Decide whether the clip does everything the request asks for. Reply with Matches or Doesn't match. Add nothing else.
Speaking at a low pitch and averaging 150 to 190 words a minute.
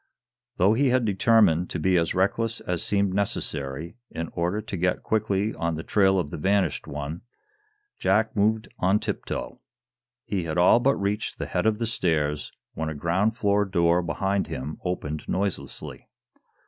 Matches